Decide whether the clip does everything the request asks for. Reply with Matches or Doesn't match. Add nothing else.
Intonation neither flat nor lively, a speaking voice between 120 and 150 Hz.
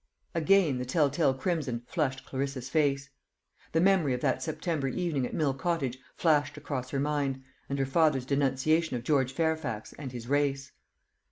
Matches